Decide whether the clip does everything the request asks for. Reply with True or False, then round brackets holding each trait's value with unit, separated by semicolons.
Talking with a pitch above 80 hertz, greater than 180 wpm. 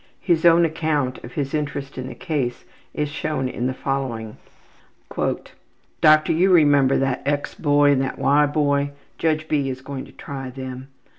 False (140 Hz; 165 wpm)